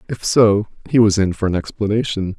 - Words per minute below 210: Yes, average, 200 wpm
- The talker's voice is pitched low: Yes, low, 100 Hz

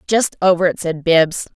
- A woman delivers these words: Yes, female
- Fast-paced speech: No, average, 190 wpm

